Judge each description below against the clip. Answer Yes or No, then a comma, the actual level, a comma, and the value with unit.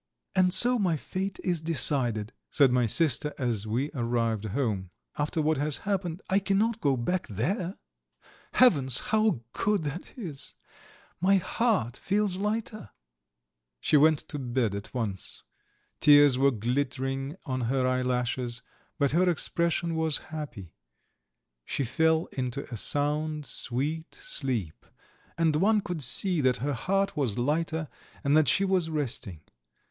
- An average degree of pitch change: No, wide, 5.9 semitones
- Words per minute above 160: No, average, 140 wpm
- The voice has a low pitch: No, medium, 145 Hz